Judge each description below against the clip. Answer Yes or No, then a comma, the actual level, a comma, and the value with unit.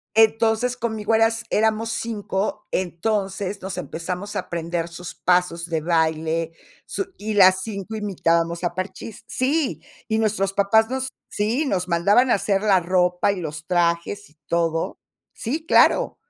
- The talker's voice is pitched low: No, high, 195 Hz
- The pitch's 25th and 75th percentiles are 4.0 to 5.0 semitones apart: Yes, average, 4.4 semitones